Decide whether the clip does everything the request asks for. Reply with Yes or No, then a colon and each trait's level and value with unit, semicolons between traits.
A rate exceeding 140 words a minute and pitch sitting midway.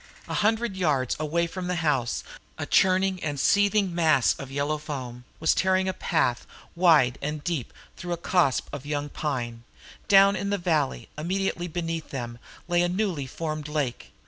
Yes: average, 170 wpm; medium, 160 Hz